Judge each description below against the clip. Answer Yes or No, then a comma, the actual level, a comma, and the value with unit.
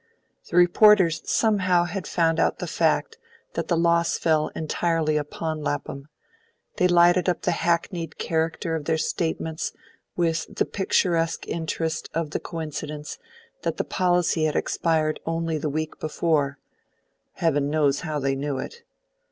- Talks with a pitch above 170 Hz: No, medium, 165 Hz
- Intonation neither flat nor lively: No, narrow, 2.0 semitones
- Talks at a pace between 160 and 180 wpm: No, average, 145 wpm